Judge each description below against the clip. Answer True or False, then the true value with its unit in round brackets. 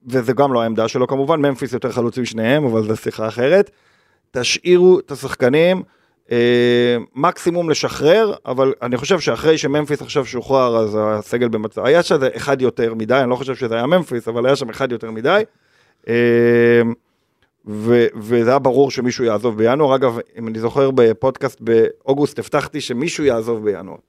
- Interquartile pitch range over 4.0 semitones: False (3.1 semitones)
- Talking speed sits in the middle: False (160 wpm)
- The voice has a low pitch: True (125 Hz)